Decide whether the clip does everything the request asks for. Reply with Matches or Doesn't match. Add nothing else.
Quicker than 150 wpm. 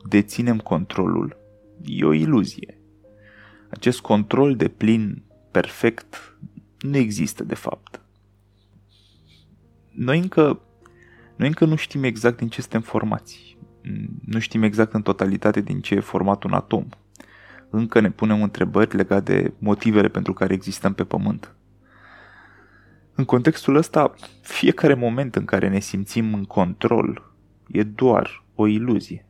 Doesn't match